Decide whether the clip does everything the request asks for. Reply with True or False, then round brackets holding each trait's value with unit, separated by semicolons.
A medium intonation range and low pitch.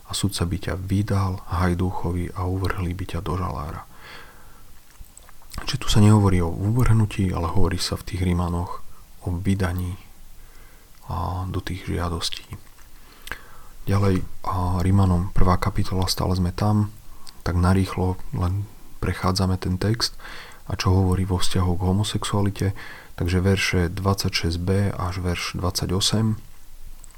False (1.9 semitones; 95 Hz)